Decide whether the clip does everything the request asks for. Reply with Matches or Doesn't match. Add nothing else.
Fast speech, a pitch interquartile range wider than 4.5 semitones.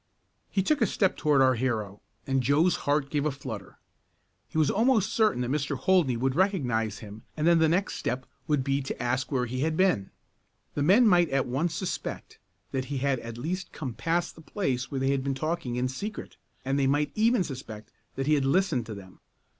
Matches